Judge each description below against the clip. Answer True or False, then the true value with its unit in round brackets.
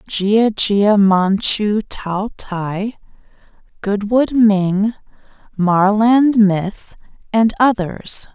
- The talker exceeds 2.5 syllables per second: False (2.4 syllables/s)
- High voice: True (205 Hz)